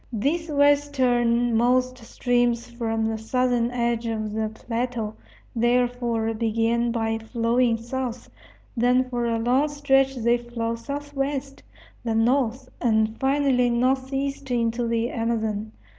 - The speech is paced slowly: Yes, slow, 115 wpm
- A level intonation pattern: Yes, narrow, 2.2 semitones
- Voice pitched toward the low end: No, high, 240 Hz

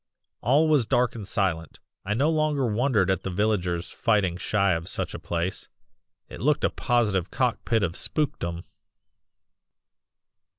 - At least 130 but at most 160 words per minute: Yes, average, 145 wpm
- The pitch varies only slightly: No, wide, 5.5 semitones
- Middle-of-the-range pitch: No, low, 105 Hz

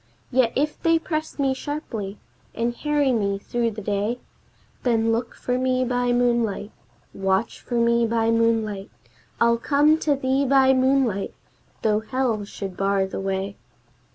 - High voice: Yes, high, 235 Hz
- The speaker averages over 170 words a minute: No, average, 150 wpm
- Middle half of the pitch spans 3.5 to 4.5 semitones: Yes, average, 3.9 semitones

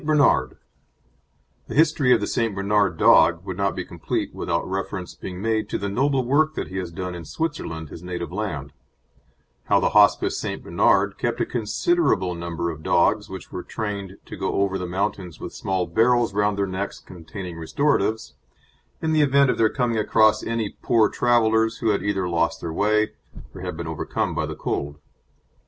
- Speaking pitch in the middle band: No, low, 100 Hz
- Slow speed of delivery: No, average, 185 wpm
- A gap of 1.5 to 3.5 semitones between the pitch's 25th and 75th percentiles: No, average, 4.2 semitones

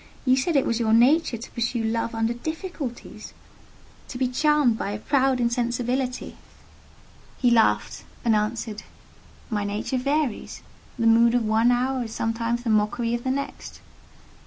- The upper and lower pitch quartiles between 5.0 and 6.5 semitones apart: No, narrow, 2.4 semitones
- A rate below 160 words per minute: Yes, average, 150 wpm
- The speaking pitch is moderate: No, high, 240 Hz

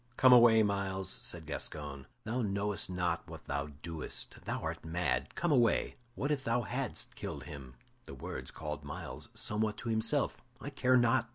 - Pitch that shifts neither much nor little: No, wide, 7.2 semitones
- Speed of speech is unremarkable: Yes, average, 170 wpm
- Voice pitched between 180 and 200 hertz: No, low, 100 Hz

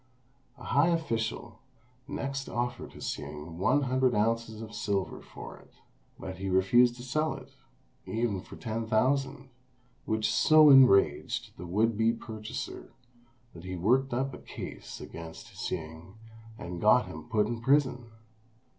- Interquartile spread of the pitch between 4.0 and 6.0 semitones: Yes, average, 4.7 semitones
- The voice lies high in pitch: No, low, 115 Hz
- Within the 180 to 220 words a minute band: No, average, 140 wpm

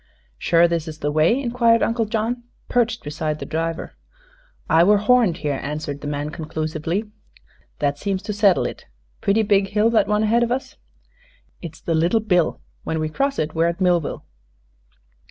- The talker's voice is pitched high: No, medium, 180 Hz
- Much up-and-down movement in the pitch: Yes, wide, 5.8 semitones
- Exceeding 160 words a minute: Yes, average, 175 wpm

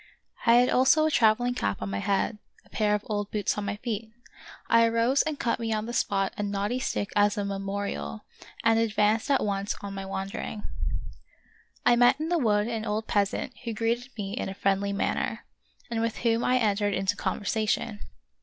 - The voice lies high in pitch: Yes, high, 215 Hz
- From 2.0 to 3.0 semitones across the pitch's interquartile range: Yes, narrow, 2.5 semitones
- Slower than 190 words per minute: No, average, 195 wpm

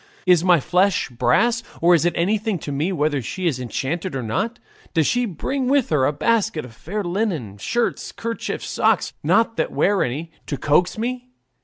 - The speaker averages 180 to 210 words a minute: Yes, average, 185 wpm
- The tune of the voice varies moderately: No, wide, 7.3 semitones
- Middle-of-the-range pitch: Yes, medium, 175 Hz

